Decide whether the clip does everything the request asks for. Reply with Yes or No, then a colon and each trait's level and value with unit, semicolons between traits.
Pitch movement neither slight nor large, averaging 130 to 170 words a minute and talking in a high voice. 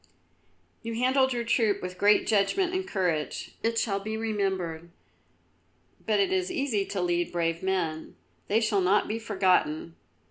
Yes: average, 4.2 semitones; average, 150 wpm; high, 205 Hz